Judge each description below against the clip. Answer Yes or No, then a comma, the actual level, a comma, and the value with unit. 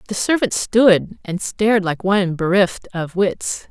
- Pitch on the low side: No, high, 195 Hz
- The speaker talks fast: No, average, 160 wpm